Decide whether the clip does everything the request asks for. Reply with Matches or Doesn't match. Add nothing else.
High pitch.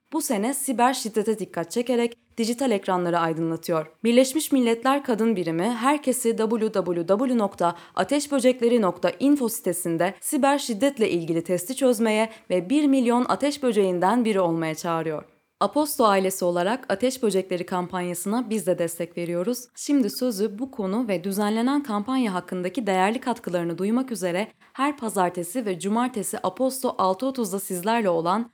Matches